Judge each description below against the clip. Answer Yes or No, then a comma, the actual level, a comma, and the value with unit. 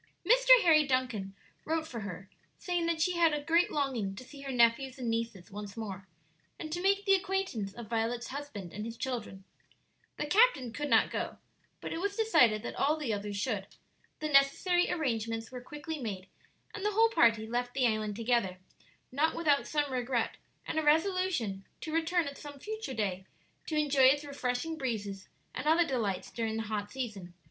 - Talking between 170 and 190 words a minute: Yes, average, 185 wpm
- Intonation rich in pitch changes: Yes, wide, 6.3 semitones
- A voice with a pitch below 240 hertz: No, very high, 260 Hz